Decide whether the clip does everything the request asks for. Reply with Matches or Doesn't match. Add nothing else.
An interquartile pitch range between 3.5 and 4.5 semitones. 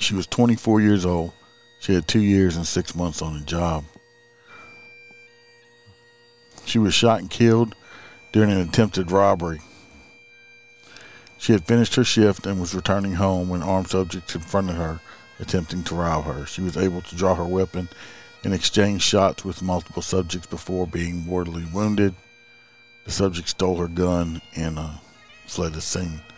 Matches